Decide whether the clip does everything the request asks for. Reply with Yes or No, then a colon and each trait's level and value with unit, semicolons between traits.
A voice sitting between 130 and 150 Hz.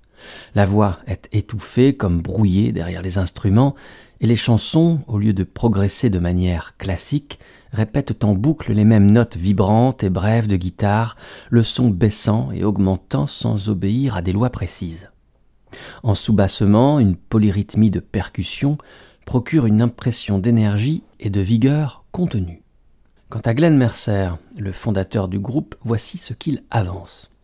No: low, 105 Hz